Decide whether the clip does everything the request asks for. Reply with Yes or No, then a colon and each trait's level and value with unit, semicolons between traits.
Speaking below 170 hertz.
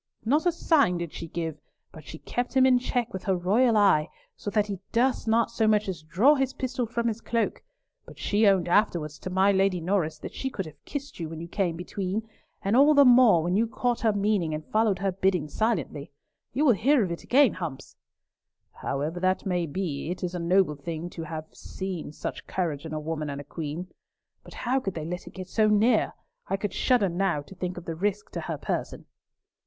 No: high, 190 Hz